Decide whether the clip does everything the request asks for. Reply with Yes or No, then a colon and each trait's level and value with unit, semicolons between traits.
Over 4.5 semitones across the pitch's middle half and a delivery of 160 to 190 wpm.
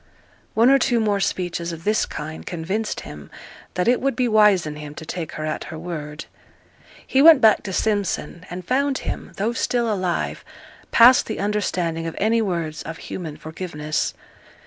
Yes: wide, 5.5 semitones; average, 175 wpm